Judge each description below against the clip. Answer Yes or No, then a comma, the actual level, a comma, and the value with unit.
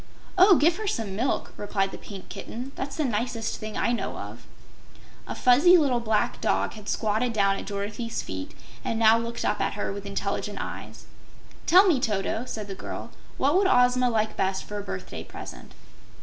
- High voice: Yes, high, 225 Hz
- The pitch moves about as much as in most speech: Yes, average, 3.7 semitones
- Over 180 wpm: Yes, average, 190 wpm